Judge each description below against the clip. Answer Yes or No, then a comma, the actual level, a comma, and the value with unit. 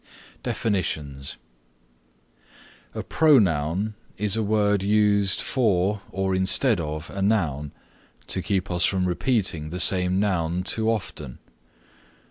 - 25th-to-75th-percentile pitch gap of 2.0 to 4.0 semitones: Yes, average, 3.2 semitones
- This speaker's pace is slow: Yes, slow, 110 wpm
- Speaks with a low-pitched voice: Yes, very low, 95 Hz